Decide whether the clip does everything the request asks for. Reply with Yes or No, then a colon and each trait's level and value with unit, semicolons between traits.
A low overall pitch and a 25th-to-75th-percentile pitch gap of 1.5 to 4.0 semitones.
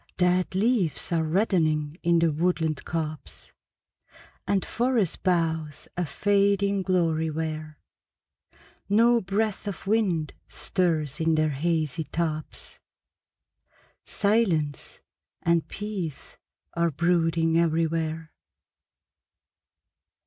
No: medium, 170 Hz; average, 3.5 semitones